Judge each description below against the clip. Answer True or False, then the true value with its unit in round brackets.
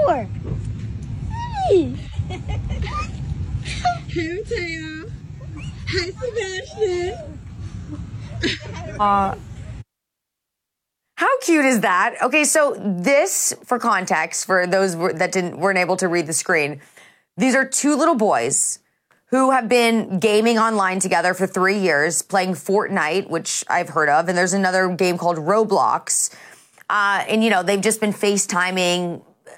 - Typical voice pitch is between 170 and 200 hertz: True (190 Hz)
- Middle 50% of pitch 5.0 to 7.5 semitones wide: True (5.6 semitones)